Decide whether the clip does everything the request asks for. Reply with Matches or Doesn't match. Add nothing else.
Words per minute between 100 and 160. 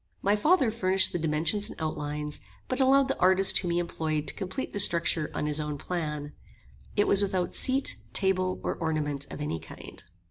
Doesn't match